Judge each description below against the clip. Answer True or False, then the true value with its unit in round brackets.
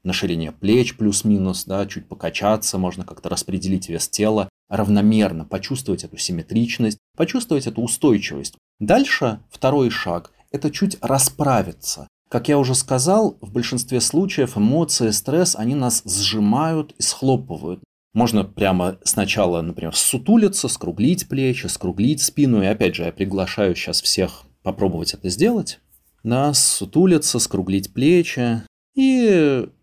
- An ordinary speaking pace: True (130 wpm)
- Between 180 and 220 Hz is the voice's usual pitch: False (115 Hz)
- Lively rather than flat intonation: True (6.2 semitones)